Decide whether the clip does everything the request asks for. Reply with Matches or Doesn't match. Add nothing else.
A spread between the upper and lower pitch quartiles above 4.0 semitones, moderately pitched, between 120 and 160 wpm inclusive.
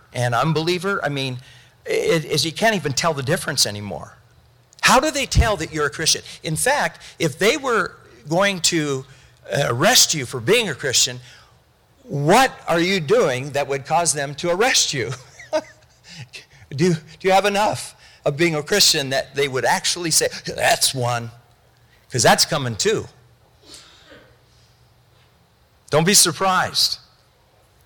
Matches